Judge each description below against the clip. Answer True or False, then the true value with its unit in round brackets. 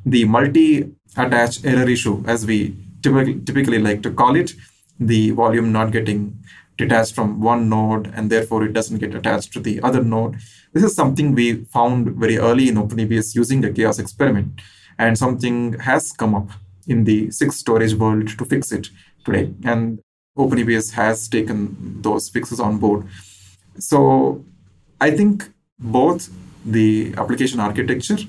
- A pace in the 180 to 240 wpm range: False (155 wpm)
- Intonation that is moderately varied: False (2.3 semitones)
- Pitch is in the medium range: False (115 Hz)